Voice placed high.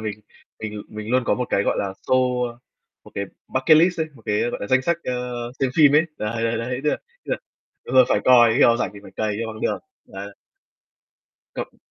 No: low, 120 Hz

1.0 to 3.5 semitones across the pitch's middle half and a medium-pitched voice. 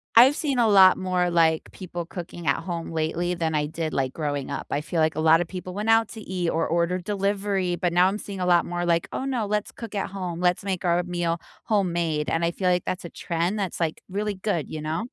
Yes: average, 2.8 semitones; medium, 175 Hz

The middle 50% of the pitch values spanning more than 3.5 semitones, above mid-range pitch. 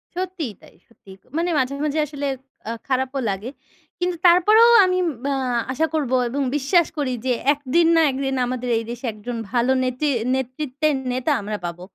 Yes: average, 4.1 semitones; very high, 270 Hz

